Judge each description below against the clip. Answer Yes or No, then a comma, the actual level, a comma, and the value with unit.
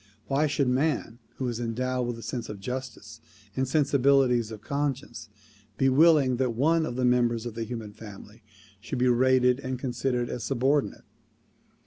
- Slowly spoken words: No, average, 165 wpm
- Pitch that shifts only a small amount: Yes, narrow, 2.3 semitones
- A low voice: Yes, low, 125 Hz